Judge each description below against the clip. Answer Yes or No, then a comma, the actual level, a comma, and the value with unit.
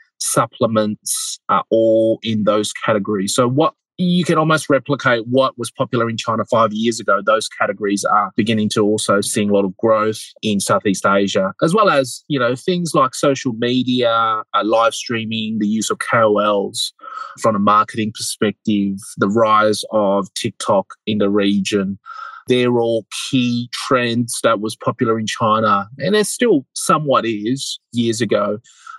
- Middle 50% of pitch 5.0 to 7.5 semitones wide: No, average, 3.7 semitones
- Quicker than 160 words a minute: No, average, 155 wpm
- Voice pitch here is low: Yes, low, 115 Hz